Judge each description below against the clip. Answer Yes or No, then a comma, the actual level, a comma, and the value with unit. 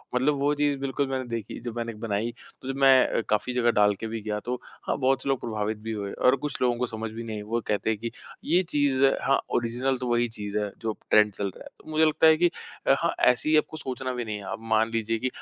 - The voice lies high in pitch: No, low, 120 Hz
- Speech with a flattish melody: No, average, 3.4 semitones